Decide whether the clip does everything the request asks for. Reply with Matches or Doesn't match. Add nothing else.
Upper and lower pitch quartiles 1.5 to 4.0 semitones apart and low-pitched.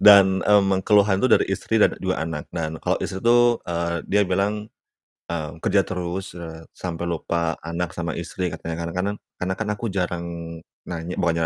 Matches